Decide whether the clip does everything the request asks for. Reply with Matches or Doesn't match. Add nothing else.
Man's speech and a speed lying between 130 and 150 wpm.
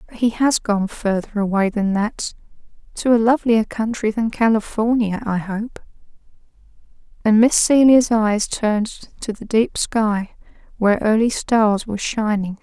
Doesn't match